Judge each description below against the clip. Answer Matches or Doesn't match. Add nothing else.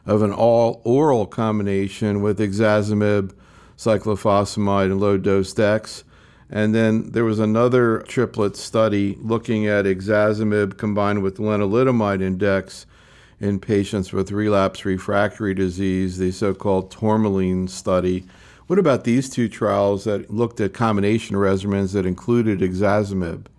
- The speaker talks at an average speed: Doesn't match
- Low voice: Matches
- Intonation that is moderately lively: Doesn't match